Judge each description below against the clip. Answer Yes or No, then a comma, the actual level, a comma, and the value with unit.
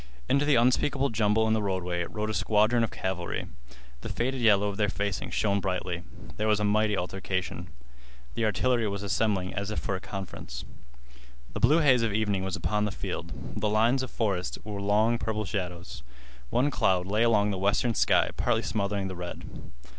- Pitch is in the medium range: No, low, 105 Hz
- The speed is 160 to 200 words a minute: Yes, average, 185 wpm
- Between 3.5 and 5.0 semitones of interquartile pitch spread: No, average, 2.8 semitones